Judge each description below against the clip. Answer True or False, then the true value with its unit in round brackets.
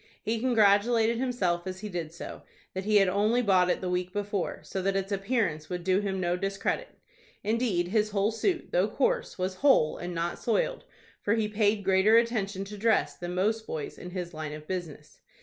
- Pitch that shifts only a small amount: False (3.5 semitones)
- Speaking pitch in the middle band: False (195 Hz)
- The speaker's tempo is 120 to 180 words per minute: False (200 wpm)